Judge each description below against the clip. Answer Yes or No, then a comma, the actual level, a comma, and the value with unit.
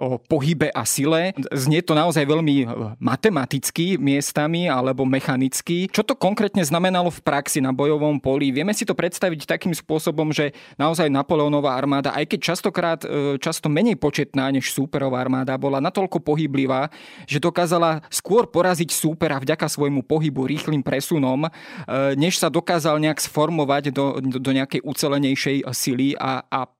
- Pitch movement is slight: No, average, 3.5 semitones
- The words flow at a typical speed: Yes, average, 150 wpm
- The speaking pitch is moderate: Yes, medium, 150 Hz